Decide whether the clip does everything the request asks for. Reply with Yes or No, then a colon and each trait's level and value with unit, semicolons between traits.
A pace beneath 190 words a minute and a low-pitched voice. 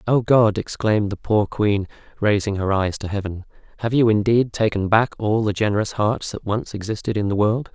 No: average, 200 wpm; low, 105 Hz